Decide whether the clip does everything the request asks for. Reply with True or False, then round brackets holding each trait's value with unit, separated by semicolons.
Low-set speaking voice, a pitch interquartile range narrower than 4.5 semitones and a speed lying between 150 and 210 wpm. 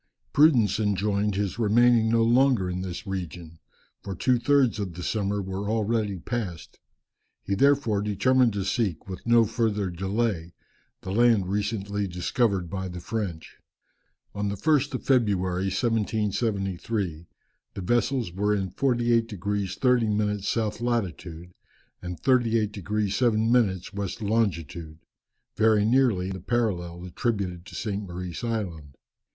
False (105 Hz; 3.8 semitones; 135 wpm)